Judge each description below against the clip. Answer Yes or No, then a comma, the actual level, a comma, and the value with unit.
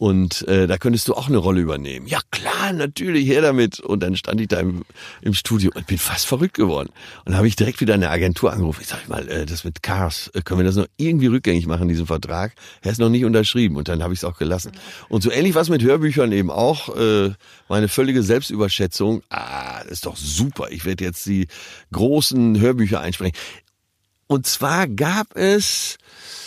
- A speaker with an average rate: No, fast, 210 wpm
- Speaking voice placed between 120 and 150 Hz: No, low, 100 Hz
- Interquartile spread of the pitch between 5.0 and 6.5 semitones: Yes, average, 5.3 semitones